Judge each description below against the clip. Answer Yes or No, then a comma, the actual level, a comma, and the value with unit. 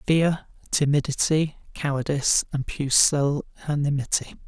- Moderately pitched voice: Yes, medium, 145 Hz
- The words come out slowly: Yes, slow, 65 wpm